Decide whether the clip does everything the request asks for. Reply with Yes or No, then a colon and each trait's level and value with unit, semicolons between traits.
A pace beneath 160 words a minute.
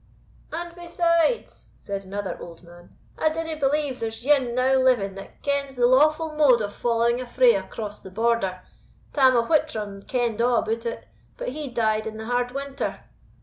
No: average, 175 wpm